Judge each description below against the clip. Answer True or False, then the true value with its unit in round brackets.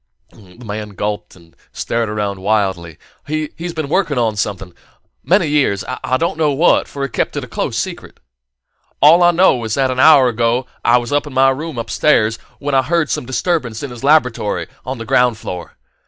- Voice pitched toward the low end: True (125 Hz)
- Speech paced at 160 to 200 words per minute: True (190 wpm)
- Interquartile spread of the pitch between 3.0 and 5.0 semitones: False (5.6 semitones)